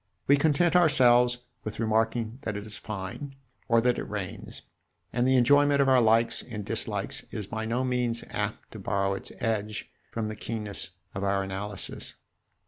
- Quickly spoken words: No, average, 170 wpm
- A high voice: No, low, 115 Hz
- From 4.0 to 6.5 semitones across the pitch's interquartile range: No, average, 3.2 semitones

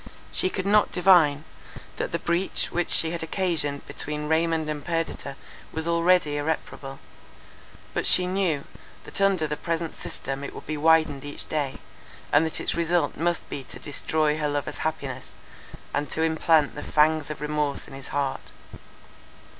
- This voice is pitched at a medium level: Yes, medium, 155 Hz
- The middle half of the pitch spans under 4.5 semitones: Yes, narrow, 2.5 semitones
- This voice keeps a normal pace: Yes, average, 160 wpm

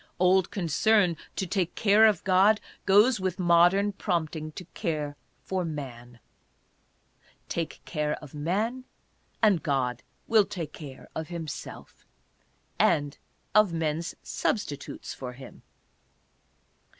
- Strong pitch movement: No, average, 4.7 semitones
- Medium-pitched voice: Yes, medium, 170 Hz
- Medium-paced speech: No, slow, 115 wpm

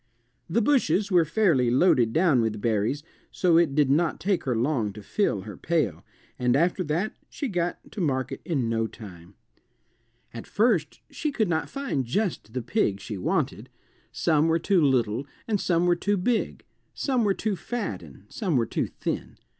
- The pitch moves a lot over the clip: Yes, wide, 8.5 semitones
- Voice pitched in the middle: Yes, medium, 155 Hz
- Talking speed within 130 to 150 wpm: No, average, 180 wpm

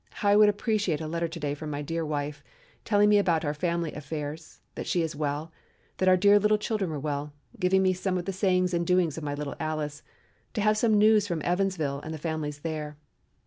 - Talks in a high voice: No, medium, 165 Hz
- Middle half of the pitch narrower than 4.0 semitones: No, average, 4.4 semitones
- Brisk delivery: Yes, fast, 225 wpm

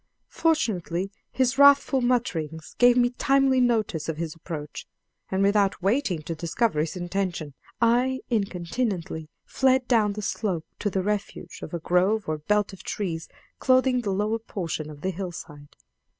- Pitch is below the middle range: No, high, 200 Hz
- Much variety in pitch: Yes, wide, 6.3 semitones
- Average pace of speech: Yes, average, 150 wpm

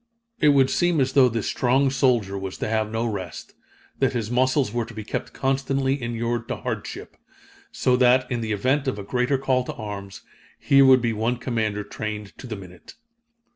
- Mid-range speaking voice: No, low, 120 Hz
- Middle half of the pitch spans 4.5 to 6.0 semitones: No, average, 3.4 semitones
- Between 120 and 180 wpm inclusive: No, average, 195 wpm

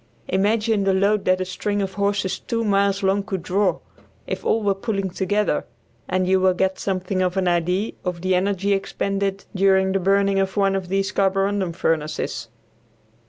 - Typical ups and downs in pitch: No, narrow, 1.2 semitones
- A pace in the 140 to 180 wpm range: Yes, average, 175 wpm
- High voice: Yes, high, 195 Hz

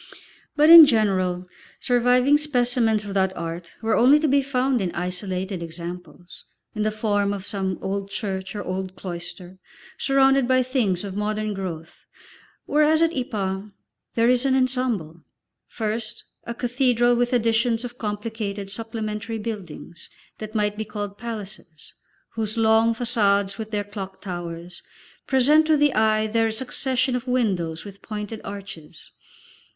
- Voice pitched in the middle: No, high, 215 Hz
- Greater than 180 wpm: No, average, 145 wpm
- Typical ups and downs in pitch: Yes, average, 4.2 semitones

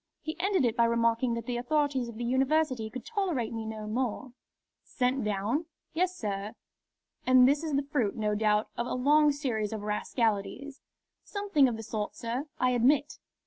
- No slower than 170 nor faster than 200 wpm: Yes, average, 180 wpm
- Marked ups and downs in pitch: No, average, 4.5 semitones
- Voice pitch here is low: No, very high, 250 Hz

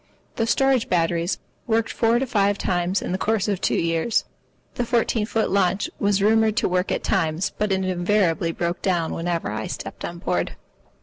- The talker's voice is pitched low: No, high, 195 Hz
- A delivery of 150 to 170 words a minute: No, average, 185 wpm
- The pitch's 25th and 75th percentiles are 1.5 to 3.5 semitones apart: No, average, 4.2 semitones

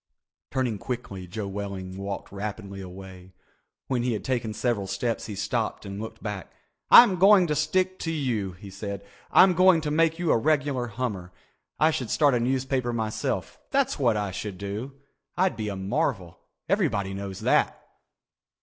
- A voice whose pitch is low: Yes, low, 110 Hz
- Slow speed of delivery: No, average, 165 wpm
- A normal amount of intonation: No, wide, 6.2 semitones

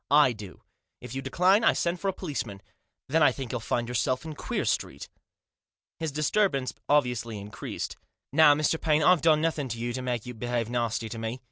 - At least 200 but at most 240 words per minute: Yes, fast, 205 wpm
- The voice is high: No, low, 130 Hz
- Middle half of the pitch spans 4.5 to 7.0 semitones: Yes, average, 4.9 semitones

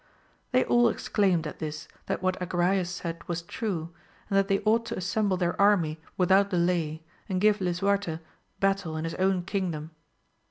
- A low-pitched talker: No, medium, 185 Hz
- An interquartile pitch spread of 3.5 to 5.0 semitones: No, average, 2.8 semitones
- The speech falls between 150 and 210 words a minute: Yes, average, 165 wpm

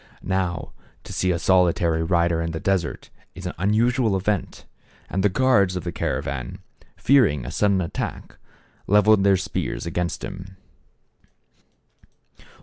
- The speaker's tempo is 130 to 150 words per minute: Yes, slow, 135 wpm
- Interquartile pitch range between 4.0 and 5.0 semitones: No, average, 2.8 semitones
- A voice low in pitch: Yes, very low, 95 Hz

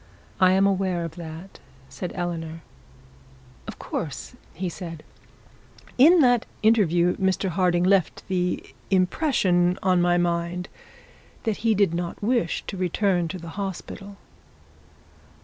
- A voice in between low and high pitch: Yes, medium, 180 Hz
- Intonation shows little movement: Yes, narrow, 2.3 semitones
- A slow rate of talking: Yes, slow, 125 wpm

